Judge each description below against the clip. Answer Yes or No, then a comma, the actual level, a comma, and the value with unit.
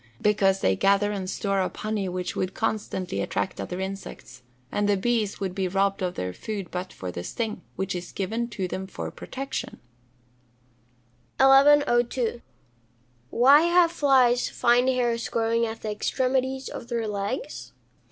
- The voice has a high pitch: Yes, high, 215 Hz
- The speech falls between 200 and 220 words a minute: No, average, 155 wpm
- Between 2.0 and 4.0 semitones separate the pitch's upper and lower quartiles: No, average, 4.4 semitones